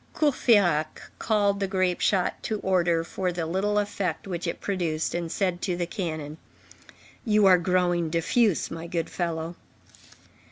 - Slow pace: No, average, 150 wpm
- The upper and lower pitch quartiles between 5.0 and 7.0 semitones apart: No, average, 2.9 semitones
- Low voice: No, medium, 180 Hz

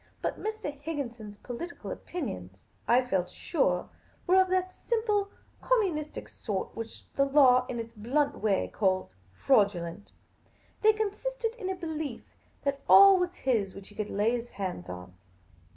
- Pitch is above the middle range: Yes, very high, 260 Hz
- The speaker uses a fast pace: No, average, 150 wpm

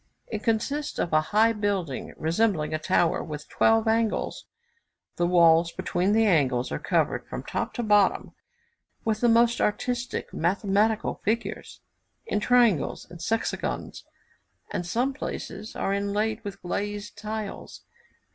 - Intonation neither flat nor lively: Yes, average, 4.3 semitones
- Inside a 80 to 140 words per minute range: Yes, slow, 135 wpm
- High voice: Yes, high, 205 Hz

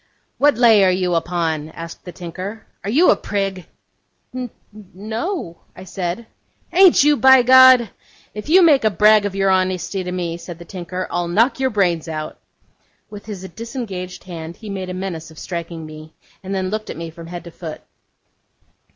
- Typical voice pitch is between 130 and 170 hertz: No, high, 190 Hz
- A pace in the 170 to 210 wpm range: Yes, average, 185 wpm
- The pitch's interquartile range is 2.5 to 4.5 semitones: Yes, average, 4.2 semitones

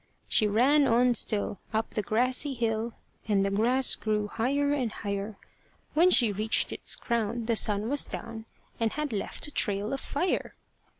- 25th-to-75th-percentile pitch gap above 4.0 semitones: No, average, 3.4 semitones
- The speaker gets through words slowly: No, average, 170 wpm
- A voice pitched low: No, high, 230 Hz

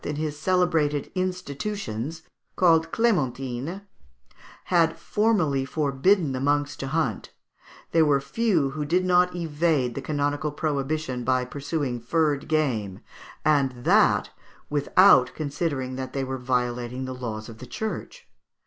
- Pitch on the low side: No, medium, 145 Hz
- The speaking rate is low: Yes, slow, 130 wpm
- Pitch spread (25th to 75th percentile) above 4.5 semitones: No, average, 4.1 semitones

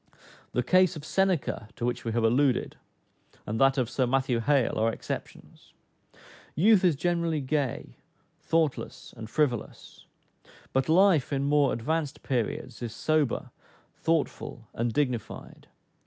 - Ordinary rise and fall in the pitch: Yes, average, 4.7 semitones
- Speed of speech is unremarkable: No, slow, 130 wpm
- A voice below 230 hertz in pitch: Yes, low, 135 Hz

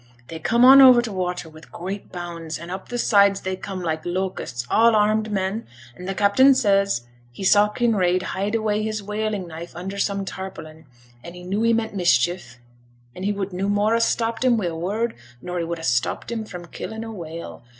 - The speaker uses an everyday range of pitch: Yes, average, 3.6 semitones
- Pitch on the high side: Yes, high, 195 Hz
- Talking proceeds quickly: Yes, fast, 210 wpm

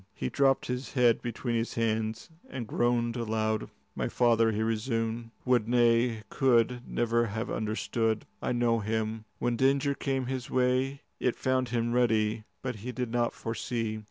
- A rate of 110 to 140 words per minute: No, average, 155 wpm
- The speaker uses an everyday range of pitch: No, narrow, 1.9 semitones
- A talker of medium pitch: No, low, 120 Hz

